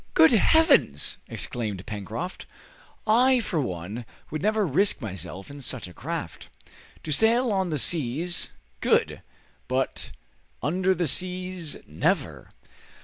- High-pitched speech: No, medium, 160 Hz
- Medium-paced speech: No, slow, 120 wpm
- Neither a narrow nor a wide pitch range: No, wide, 8.2 semitones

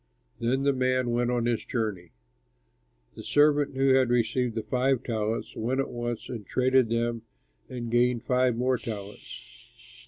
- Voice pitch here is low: Yes, low, 120 Hz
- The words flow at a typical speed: Yes, average, 155 wpm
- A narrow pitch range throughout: Yes, narrow, 1.8 semitones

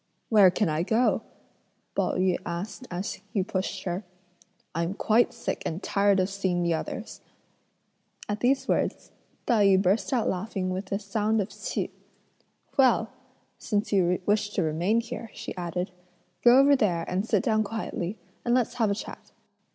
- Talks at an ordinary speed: Yes, average, 165 wpm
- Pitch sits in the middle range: No, high, 200 Hz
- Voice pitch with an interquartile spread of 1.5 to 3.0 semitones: No, average, 3.5 semitones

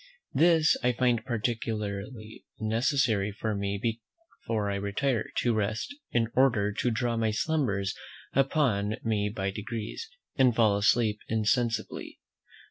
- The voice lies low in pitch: Yes, low, 110 Hz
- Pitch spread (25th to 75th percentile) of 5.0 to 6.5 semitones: No, average, 3.2 semitones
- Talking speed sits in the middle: No, slow, 125 wpm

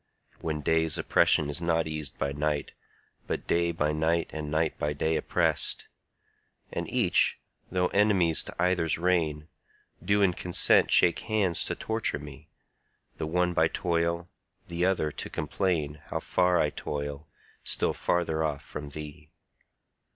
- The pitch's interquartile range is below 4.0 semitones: Yes, narrow, 2.6 semitones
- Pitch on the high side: No, very low, 80 Hz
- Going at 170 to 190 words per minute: No, average, 145 wpm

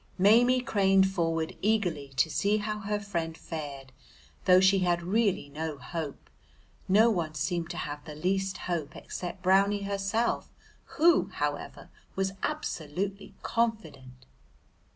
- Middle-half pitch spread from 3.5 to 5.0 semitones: Yes, average, 4.2 semitones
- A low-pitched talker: No, medium, 185 Hz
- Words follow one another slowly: Yes, slow, 130 wpm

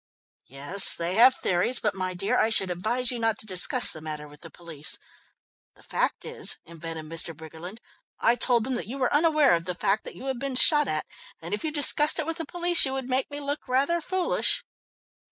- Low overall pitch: No, high, 235 Hz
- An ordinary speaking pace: No, fast, 220 wpm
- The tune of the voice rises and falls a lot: Yes, wide, 8.2 semitones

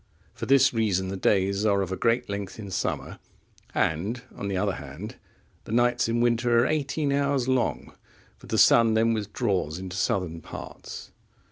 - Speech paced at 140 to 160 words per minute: No, average, 170 wpm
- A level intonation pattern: No, average, 4.2 semitones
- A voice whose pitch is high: No, low, 110 Hz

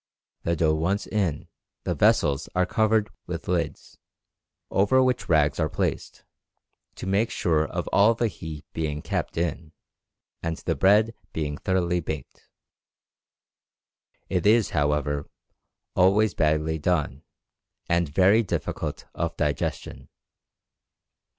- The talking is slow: Yes, slow, 120 wpm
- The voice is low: Yes, very low, 85 Hz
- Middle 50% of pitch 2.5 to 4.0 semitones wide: No, average, 4.5 semitones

